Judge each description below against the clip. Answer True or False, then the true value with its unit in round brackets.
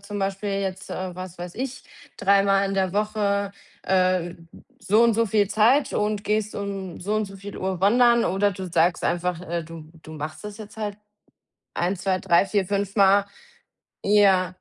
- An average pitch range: False (2.1 semitones)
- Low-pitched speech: False (195 Hz)